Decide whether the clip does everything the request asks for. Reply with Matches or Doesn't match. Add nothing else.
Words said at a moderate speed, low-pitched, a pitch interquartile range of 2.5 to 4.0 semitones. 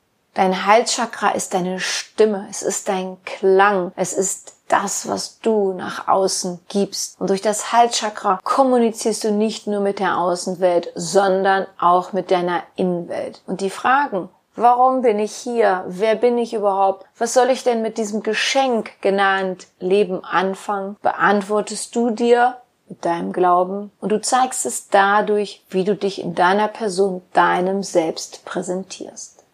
Doesn't match